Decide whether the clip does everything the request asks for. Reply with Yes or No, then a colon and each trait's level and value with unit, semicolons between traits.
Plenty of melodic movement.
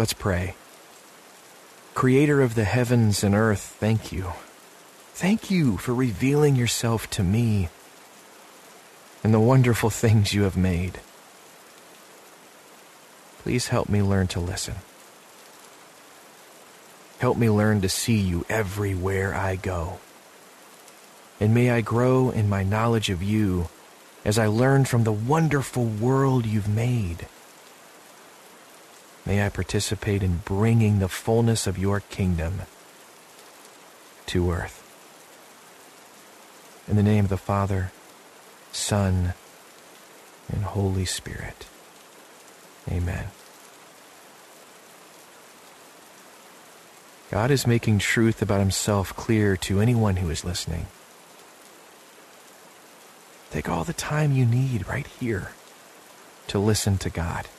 No: average, 3.6 semitones